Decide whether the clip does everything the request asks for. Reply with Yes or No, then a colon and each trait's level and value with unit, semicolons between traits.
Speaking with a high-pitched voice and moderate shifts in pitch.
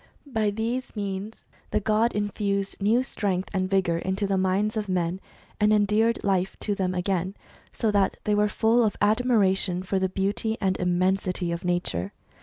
No: high, 200 Hz; narrow, 2.3 semitones